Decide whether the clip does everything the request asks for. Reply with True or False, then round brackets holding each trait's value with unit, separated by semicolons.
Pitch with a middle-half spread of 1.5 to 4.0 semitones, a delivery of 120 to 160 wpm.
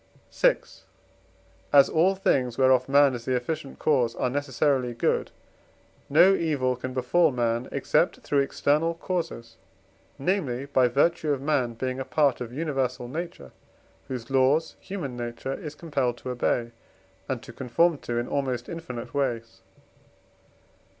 True (3.6 semitones; 140 wpm)